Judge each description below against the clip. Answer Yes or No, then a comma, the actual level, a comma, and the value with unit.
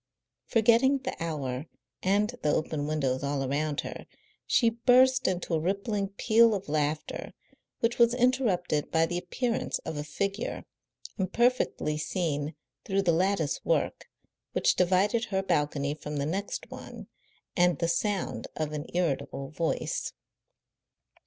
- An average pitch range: No, wide, 6.2 semitones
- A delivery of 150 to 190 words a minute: No, slow, 135 wpm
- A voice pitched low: No, medium, 180 Hz